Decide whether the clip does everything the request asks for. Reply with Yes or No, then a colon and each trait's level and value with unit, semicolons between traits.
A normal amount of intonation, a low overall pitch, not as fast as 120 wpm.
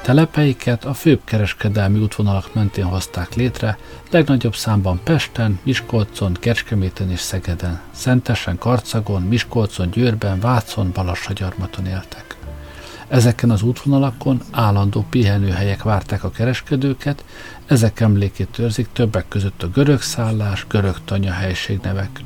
Yes: average, 4.2 semitones; low, 110 Hz; average, 110 wpm